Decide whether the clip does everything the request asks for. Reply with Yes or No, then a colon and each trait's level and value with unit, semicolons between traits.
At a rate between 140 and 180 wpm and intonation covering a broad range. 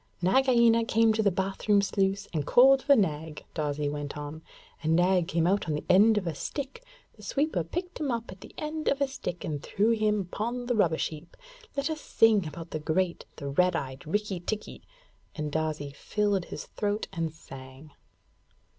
No: average, 190 wpm; wide, 6.2 semitones